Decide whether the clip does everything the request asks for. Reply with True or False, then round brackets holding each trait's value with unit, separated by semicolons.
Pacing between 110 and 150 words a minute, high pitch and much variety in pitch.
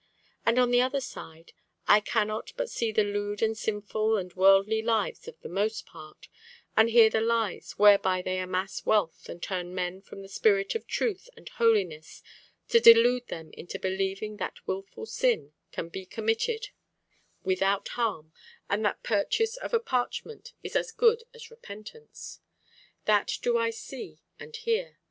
False (165 wpm; 215 Hz; 5.8 semitones)